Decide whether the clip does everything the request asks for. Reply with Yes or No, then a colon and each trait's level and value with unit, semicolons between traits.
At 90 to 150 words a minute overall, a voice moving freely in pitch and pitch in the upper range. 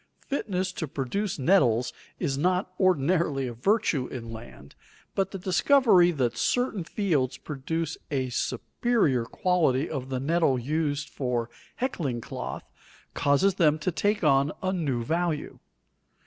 No: slow, 135 wpm; wide, 6.0 semitones; medium, 155 Hz